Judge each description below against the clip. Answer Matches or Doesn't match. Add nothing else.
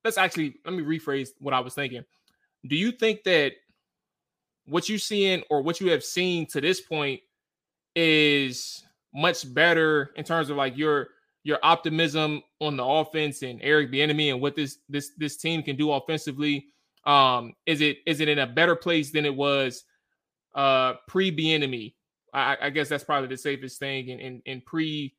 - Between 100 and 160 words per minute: Doesn't match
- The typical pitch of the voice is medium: Matches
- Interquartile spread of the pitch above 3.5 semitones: Doesn't match